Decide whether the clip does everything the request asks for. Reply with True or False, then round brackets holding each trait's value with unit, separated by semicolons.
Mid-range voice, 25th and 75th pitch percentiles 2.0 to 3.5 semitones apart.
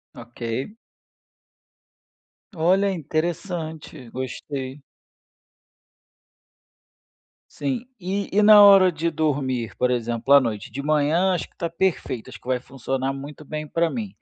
False (150 Hz; 5.5 semitones)